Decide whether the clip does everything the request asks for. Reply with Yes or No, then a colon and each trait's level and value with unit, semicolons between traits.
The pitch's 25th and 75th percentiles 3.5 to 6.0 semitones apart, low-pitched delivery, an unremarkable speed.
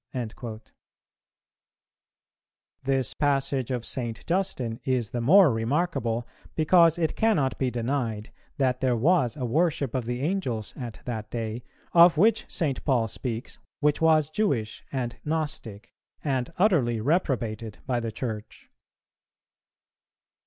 No: average, 5.1 semitones; low, 130 Hz; slow, 125 wpm